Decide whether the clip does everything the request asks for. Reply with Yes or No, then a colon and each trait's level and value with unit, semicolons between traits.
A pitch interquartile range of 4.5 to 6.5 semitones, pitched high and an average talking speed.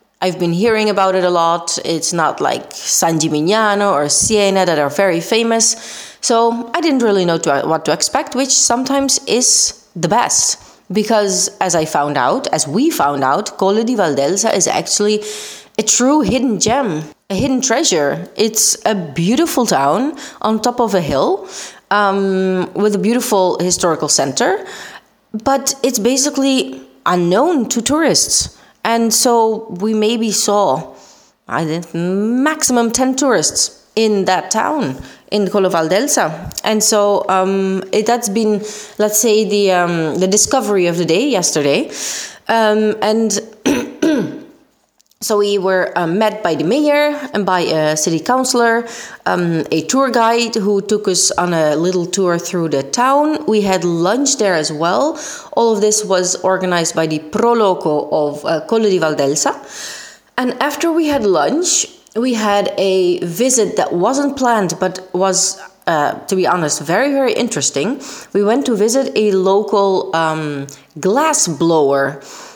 Yes: average, 5.0 semitones; high, 205 Hz; average, 150 wpm